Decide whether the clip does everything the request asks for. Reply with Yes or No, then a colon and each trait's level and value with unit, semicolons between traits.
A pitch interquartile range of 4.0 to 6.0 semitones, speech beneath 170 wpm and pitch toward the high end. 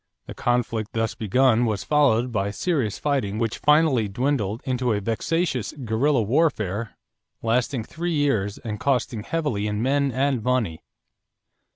No: average, 4.6 semitones; average, 140 wpm; low, 120 Hz